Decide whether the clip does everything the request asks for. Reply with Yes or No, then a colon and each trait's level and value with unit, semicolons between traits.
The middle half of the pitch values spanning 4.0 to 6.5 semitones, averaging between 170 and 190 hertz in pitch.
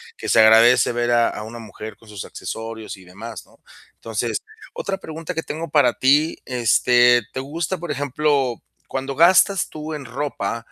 No: average, 4.9 semitones; low, 125 Hz